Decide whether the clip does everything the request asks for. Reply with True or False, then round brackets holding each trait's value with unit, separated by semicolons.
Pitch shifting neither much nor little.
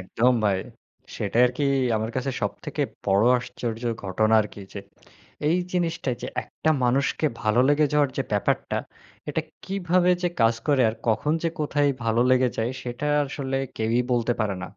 True (4.8 semitones)